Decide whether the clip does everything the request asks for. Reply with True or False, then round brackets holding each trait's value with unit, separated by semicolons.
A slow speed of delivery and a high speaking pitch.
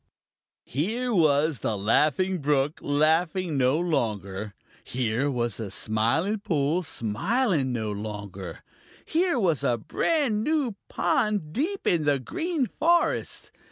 False (120 wpm; 150 Hz)